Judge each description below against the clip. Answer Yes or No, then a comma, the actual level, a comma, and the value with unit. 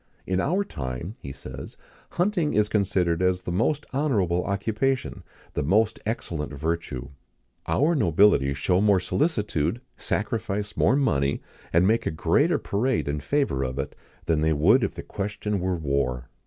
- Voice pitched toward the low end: Yes, very low, 95 Hz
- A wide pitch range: Yes, wide, 6.8 semitones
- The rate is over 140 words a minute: Yes, average, 155 wpm